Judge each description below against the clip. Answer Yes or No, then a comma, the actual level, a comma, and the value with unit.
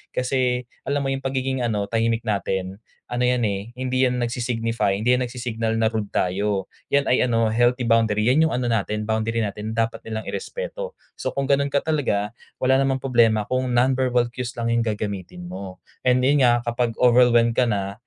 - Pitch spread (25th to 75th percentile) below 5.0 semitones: Yes, narrow, 2.6 semitones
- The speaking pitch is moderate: No, low, 120 Hz